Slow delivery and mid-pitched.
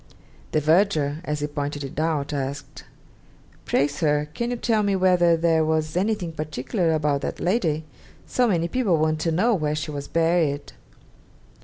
No: average, 165 wpm; medium, 160 Hz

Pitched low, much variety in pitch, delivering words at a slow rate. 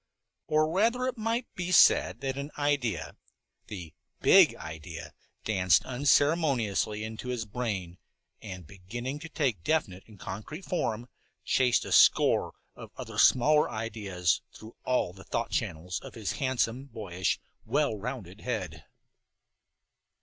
Yes: low, 115 Hz; wide, 7.1 semitones; slow, 130 wpm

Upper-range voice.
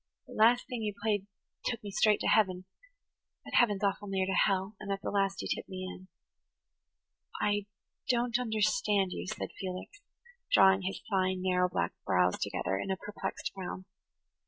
Yes: high, 195 Hz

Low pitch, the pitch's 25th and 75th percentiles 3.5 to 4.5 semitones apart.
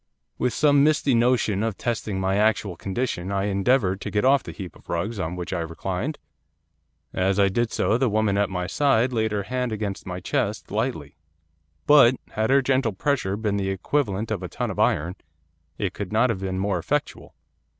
Yes: low, 105 Hz; average, 4.1 semitones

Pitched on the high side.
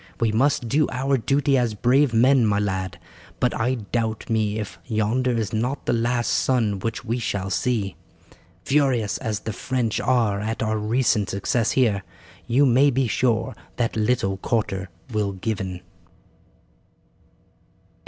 No: low, 115 Hz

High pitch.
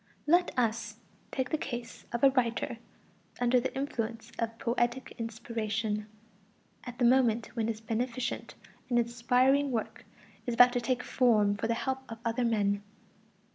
Yes: high, 235 Hz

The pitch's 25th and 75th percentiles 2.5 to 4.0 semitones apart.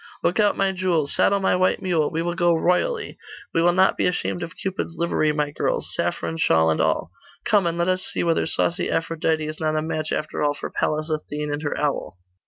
Yes: average, 3.0 semitones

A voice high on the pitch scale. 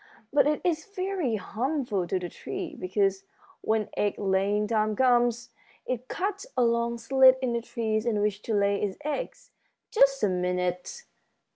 Yes: high, 230 Hz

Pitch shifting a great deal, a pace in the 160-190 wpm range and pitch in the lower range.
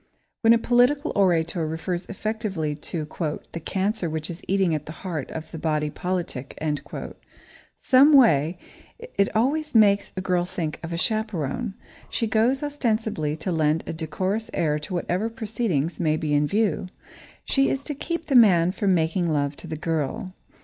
No: wide, 5.8 semitones; average, 165 wpm; medium, 185 Hz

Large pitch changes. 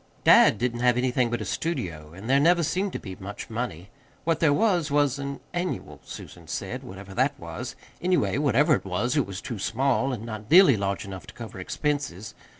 Yes: wide, 6.7 semitones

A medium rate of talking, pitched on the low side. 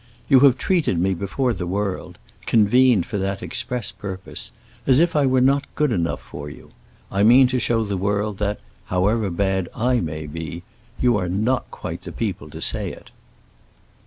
Yes: average, 170 wpm; low, 105 Hz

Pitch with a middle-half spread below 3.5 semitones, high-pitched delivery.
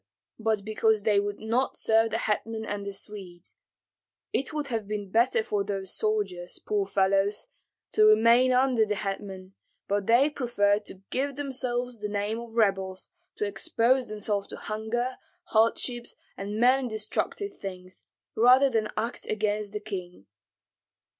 Yes: average, 2.8 semitones; high, 215 Hz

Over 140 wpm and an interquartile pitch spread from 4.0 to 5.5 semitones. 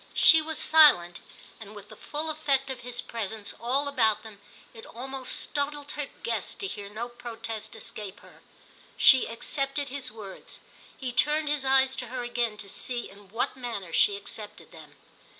Yes: average, 170 wpm; average, 4.3 semitones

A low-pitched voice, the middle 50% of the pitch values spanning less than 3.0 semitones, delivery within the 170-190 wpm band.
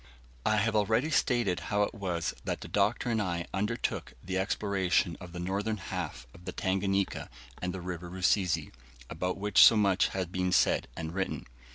Yes: very low, 95 Hz; narrow, 2.4 semitones; average, 180 wpm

